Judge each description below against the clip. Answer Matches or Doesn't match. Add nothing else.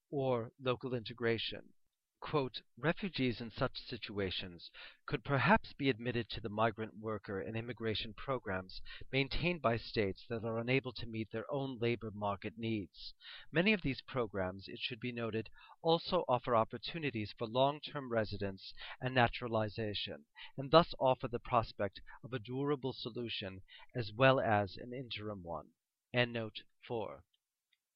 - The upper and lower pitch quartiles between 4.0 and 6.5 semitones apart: Doesn't match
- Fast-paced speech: Doesn't match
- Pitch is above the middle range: Doesn't match